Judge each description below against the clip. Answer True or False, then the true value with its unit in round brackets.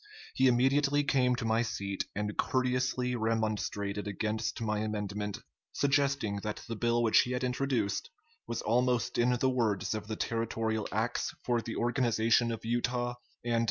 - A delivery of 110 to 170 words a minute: True (155 wpm)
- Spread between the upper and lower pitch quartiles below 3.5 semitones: True (2.5 semitones)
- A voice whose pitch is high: False (115 Hz)